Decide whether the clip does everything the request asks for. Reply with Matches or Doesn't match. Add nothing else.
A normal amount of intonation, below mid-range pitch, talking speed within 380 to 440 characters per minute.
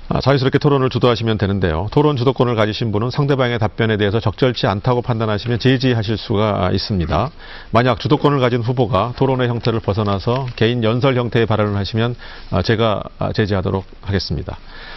Matches